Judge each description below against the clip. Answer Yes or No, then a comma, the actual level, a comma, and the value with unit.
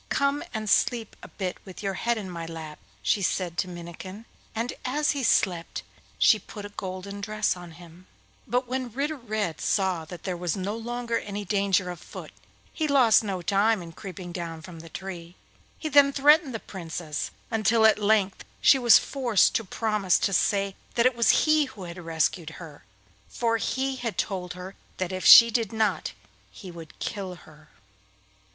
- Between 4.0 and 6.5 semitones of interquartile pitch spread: Yes, average, 4.6 semitones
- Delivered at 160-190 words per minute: Yes, average, 180 wpm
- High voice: Yes, high, 200 Hz